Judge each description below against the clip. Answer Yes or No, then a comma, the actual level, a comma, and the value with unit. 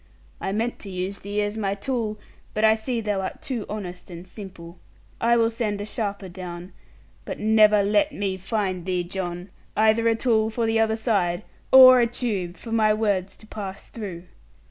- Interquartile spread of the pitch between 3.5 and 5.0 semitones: No, average, 2.9 semitones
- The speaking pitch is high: Yes, high, 210 Hz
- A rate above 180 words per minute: Yes, average, 190 wpm